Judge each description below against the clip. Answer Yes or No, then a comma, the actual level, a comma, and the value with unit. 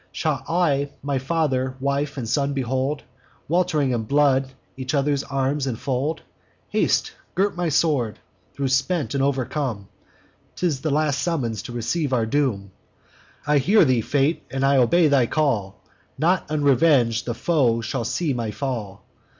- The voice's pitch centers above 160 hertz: No, medium, 140 Hz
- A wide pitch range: No, average, 3.2 semitones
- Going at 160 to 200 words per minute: No, average, 150 wpm